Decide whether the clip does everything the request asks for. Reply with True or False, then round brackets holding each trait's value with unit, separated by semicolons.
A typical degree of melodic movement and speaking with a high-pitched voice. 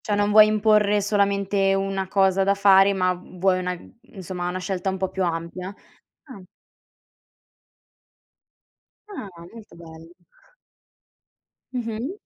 False (2.0 semitones; 195 Hz)